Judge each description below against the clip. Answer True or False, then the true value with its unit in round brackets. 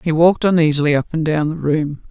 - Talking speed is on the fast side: True (230 wpm)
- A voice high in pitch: False (160 Hz)